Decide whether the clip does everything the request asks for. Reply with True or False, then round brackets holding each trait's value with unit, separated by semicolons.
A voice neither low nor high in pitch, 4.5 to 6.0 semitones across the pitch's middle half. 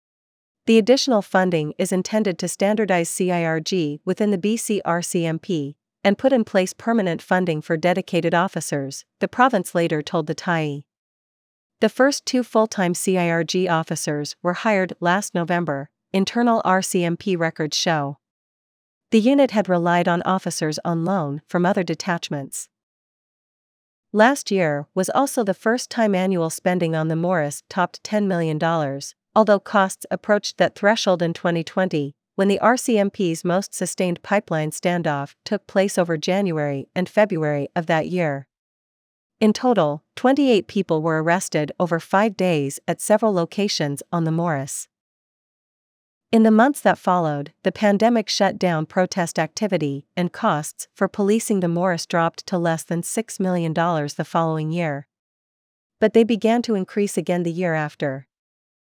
False (180 Hz; 3.9 semitones)